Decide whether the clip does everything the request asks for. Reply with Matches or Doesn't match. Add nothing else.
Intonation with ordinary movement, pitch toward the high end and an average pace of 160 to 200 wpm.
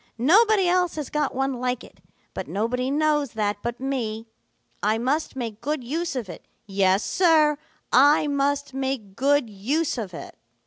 Matches